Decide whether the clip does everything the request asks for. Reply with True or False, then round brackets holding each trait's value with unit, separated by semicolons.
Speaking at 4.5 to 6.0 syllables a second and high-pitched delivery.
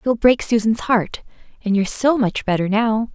True (4.9 syllables/s; 220 Hz)